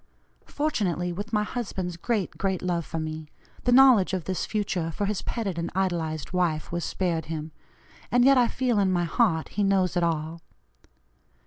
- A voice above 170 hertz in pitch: Yes, medium, 185 Hz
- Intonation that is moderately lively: Yes, average, 4.0 semitones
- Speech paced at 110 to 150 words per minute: No, average, 180 wpm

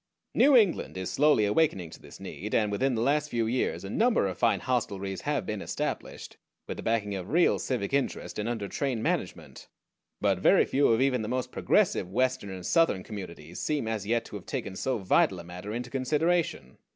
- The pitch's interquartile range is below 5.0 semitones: No, wide, 5.6 semitones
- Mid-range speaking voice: No, low, 115 Hz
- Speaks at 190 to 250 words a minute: Yes, average, 200 wpm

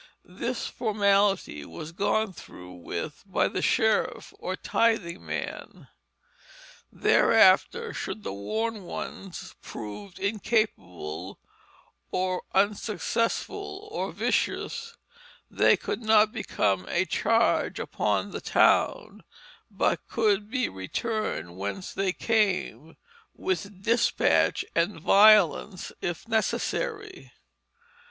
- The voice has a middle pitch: No, high, 200 Hz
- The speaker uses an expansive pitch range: No, average, 4.7 semitones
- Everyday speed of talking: No, slow, 95 wpm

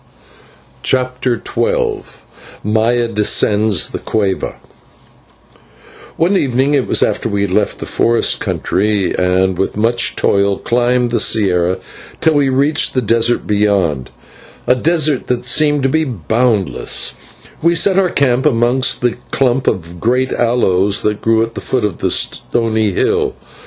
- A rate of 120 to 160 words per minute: Yes, average, 140 wpm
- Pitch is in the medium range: No, low, 120 Hz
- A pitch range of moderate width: Yes, average, 4.2 semitones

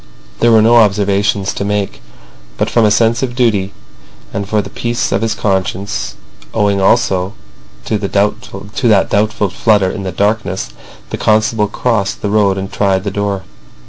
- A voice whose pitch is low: Yes, low, 105 Hz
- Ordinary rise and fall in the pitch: No, narrow, 1.9 semitones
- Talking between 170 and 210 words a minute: No, average, 160 wpm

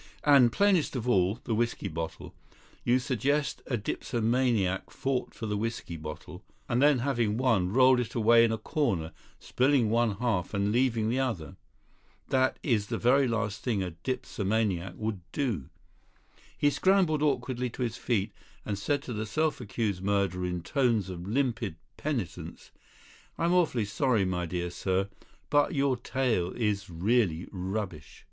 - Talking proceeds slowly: No, average, 155 wpm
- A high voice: No, low, 115 Hz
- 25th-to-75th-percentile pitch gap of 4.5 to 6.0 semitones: Yes, average, 4.9 semitones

